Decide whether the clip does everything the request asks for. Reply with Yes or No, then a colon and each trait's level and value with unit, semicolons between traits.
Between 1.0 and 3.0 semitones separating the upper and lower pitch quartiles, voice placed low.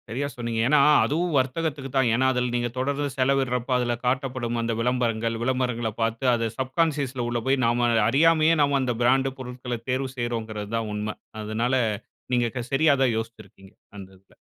Yes: narrow, 2.5 semitones; low, 125 Hz